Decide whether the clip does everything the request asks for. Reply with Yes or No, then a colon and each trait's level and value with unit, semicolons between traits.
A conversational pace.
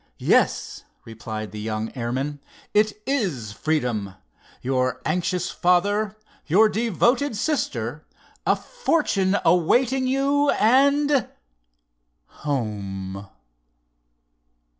No: slow, 65 wpm